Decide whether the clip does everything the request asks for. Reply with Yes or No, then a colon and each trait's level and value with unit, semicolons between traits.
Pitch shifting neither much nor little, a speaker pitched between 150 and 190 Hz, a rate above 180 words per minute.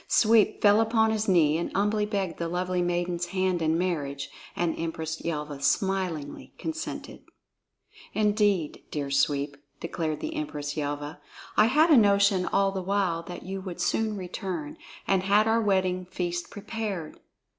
No: average, 4.1 semitones; medium, 185 Hz; average, 150 wpm